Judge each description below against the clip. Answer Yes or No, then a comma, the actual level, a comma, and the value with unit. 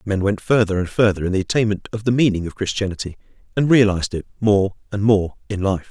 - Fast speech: Yes, fast, 215 wpm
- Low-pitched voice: Yes, low, 100 Hz